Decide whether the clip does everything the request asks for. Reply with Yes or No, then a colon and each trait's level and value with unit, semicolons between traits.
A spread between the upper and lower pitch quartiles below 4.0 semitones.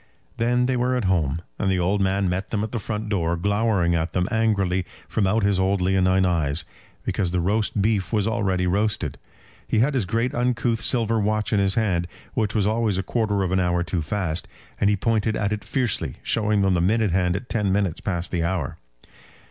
Yes: average, 3.3 semitones